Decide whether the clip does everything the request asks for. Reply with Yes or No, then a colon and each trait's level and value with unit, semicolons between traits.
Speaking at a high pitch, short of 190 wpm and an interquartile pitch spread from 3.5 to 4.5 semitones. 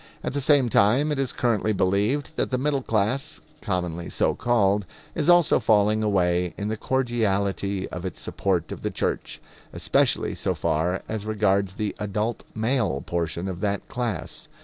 No: low, 105 Hz; average, 165 wpm; average, 4.1 semitones